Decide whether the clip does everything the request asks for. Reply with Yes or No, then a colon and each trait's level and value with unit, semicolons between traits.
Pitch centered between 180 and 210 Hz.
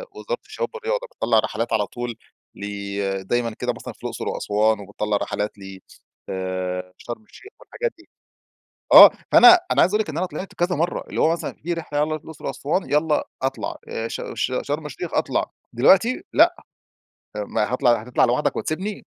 No: medium, 140 Hz